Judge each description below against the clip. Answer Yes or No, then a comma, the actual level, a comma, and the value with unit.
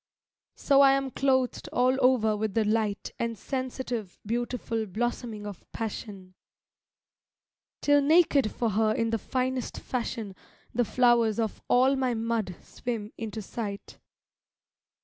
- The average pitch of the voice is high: Yes, high, 230 Hz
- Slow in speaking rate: Yes, slow, 130 wpm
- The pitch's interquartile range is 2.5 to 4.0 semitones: Yes, average, 3.0 semitones